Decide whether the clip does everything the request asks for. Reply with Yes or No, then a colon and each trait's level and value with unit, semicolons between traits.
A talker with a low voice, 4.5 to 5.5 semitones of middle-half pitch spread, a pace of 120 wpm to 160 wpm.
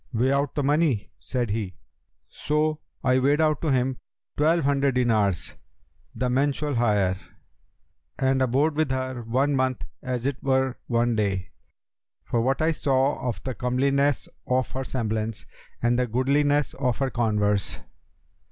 No: low, 130 Hz; average, 2.9 semitones; average, 145 wpm